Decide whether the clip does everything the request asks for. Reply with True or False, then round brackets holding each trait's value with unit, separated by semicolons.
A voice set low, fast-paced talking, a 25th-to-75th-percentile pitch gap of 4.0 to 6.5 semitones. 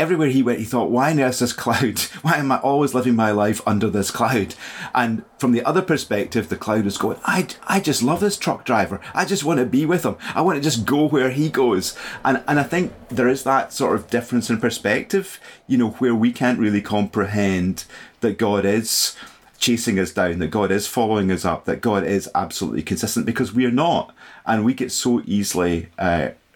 True (120 Hz; 215 wpm; 4.3 semitones)